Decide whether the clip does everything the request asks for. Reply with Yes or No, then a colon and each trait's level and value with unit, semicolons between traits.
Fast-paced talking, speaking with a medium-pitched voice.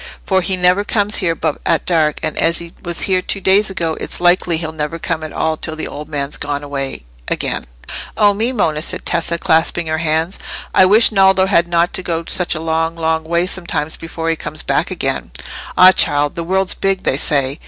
Yes: fast, 215 wpm; medium, 170 Hz